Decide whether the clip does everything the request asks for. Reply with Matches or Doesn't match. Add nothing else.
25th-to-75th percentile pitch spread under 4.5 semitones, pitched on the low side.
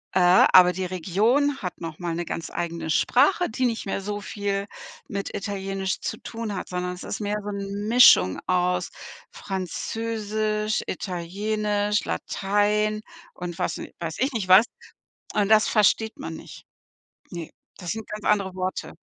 Doesn't match